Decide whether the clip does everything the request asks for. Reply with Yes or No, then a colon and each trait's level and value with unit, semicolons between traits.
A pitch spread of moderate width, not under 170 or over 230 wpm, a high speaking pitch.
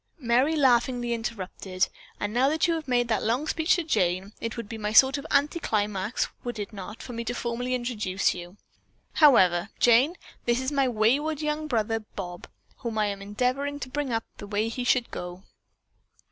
Yes: average, 4.4 semitones; average, 195 wpm; high, 235 Hz